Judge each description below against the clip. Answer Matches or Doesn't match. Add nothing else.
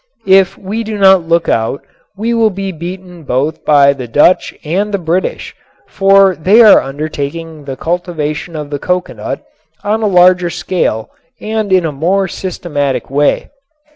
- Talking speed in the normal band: Matches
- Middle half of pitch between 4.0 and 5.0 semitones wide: Matches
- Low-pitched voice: Doesn't match